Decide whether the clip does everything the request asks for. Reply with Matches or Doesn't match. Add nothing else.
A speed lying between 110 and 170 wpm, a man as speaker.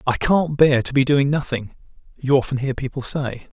Doesn't match